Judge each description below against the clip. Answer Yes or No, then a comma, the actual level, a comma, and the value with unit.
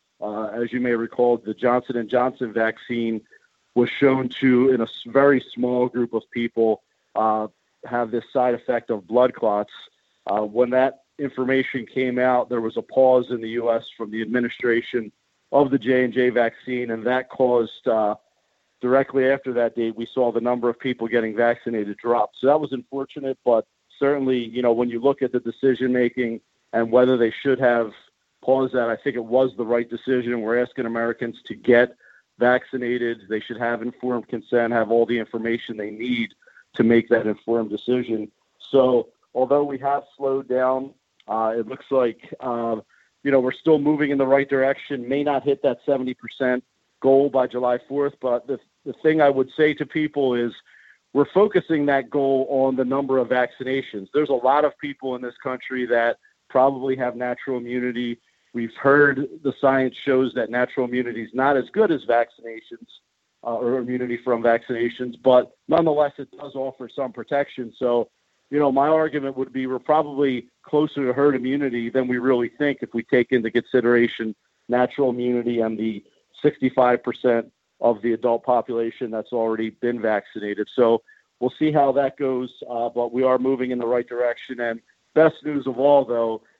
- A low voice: Yes, low, 125 Hz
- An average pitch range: No, narrow, 2.2 semitones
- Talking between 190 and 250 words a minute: No, average, 180 wpm